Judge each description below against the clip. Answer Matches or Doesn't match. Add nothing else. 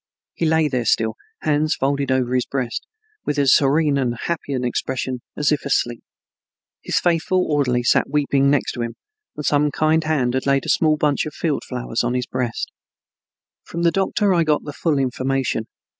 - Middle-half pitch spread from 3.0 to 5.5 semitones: Matches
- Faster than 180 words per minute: Matches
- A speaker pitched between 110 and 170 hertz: Matches